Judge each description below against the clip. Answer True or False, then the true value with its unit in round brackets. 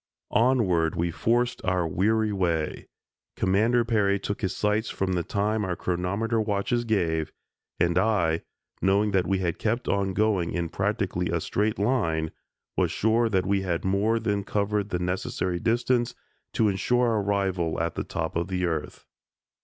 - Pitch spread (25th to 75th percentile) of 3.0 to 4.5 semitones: True (3.7 semitones)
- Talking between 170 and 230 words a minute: False (160 wpm)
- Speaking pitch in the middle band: False (100 Hz)